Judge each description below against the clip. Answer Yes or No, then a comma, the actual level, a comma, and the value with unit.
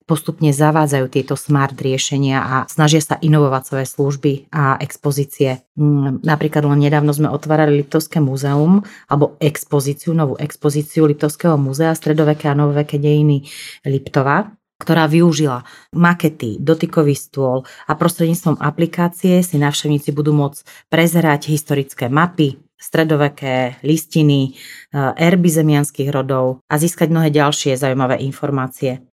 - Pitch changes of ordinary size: No, narrow, 2.3 semitones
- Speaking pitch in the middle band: Yes, medium, 150 Hz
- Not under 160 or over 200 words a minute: No, average, 115 wpm